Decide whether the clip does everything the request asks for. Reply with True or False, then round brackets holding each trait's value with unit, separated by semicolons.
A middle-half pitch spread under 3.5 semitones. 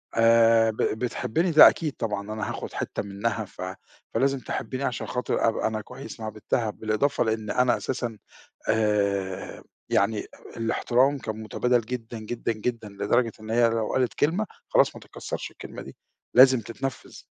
True (2.6 semitones)